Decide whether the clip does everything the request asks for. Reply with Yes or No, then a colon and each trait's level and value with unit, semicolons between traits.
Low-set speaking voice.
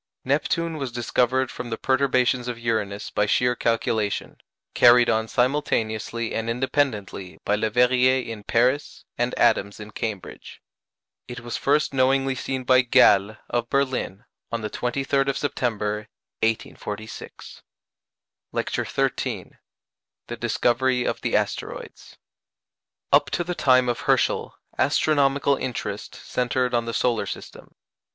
Yes: low, 125 Hz